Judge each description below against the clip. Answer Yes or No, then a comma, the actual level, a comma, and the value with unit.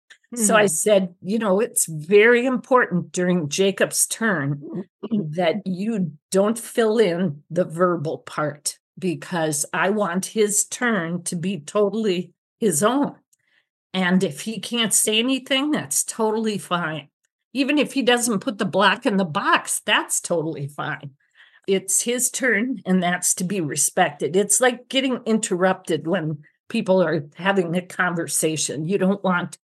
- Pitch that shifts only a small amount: No, average, 4.1 semitones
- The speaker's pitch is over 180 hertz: Yes, high, 190 Hz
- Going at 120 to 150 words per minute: Yes, average, 145 wpm